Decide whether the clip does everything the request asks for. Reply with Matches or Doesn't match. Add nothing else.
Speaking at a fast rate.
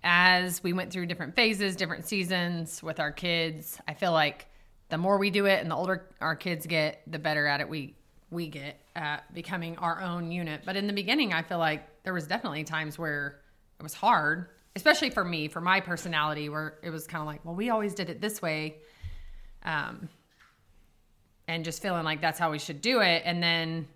Matches